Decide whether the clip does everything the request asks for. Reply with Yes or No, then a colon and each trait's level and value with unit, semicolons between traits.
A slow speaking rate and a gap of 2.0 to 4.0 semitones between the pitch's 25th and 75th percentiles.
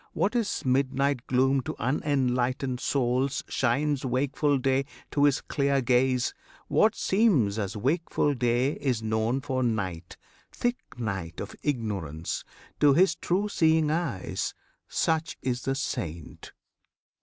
Yes: slow, 125 wpm; average, 3.5 semitones